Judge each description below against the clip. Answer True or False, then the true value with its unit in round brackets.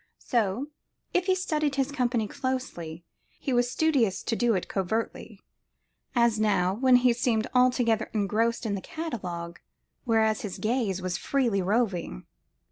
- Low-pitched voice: False (230 Hz)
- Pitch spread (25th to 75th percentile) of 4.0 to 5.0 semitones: True (4.3 semitones)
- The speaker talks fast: False (140 wpm)